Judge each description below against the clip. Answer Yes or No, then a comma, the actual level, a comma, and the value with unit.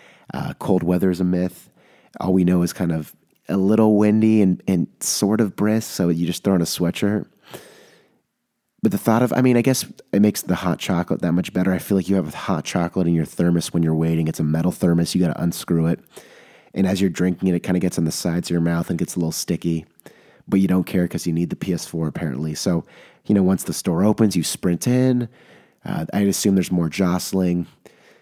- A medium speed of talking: No, fast, 240 wpm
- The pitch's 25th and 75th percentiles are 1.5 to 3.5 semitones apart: Yes, narrow, 2.6 semitones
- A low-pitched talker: Yes, very low, 90 Hz